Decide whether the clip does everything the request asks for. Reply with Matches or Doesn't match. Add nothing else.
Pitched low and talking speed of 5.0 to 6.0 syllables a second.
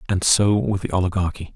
Matches